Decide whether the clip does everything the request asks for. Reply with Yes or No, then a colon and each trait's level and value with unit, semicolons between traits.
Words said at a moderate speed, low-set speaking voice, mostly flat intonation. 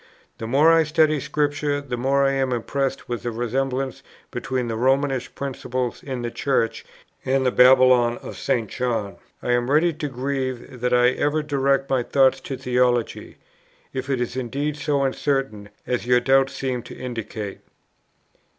Yes: average, 165 wpm; low, 130 Hz; narrow, 2.1 semitones